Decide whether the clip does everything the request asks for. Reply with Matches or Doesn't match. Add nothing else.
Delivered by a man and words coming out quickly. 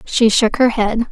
Doesn't match